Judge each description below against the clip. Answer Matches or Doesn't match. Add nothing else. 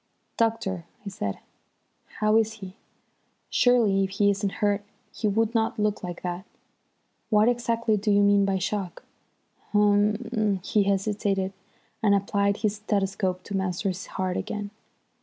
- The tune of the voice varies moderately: Doesn't match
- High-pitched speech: Matches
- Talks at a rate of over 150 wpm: Doesn't match